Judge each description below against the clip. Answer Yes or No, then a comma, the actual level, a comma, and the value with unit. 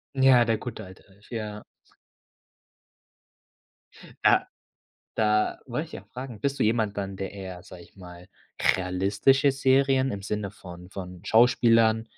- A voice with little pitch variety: No, average, 4.1 semitones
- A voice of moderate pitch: No, low, 105 Hz